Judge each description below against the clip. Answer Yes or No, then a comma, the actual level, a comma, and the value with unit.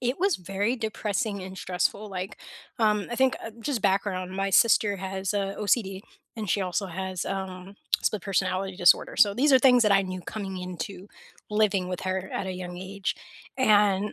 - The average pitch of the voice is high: Yes, high, 195 Hz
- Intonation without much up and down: Yes, narrow, 2.2 semitones